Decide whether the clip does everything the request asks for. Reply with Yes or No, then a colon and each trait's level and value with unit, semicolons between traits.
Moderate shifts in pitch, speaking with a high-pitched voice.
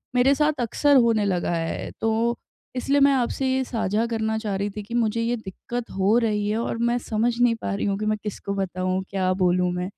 Yes: average, 3.5 semitones; high, 220 Hz